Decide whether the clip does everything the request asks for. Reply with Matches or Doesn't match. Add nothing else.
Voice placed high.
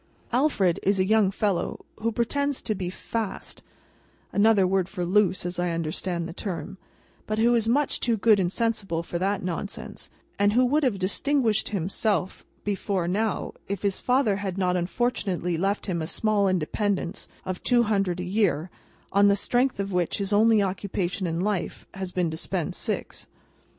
Matches